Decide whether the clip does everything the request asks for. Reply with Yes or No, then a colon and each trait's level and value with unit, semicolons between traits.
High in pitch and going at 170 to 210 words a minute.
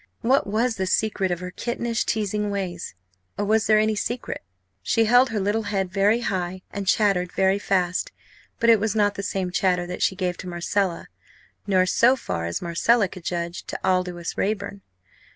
Yes: high, 200 Hz; average, 185 wpm